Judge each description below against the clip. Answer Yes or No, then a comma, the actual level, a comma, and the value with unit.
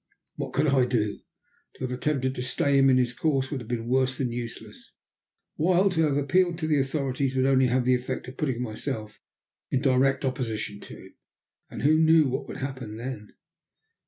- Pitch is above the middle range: No, low, 130 Hz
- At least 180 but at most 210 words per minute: Yes, average, 200 wpm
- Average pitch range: No, narrow, 2.3 semitones